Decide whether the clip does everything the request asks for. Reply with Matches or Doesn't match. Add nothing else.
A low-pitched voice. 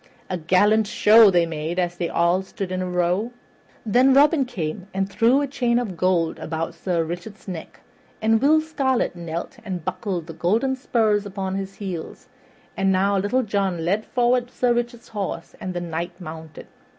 Doesn't match